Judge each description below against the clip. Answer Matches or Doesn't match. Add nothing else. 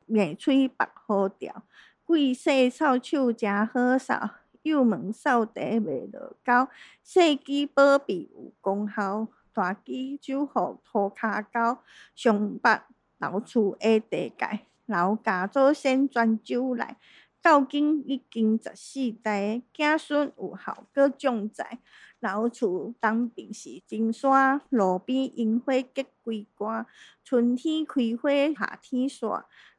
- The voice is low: Doesn't match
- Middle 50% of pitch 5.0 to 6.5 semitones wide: Doesn't match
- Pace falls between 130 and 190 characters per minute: Matches